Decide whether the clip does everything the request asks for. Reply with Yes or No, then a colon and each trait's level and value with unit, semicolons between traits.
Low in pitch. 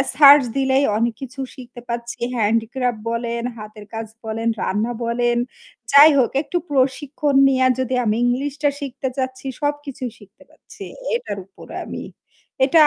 No: very high, 255 Hz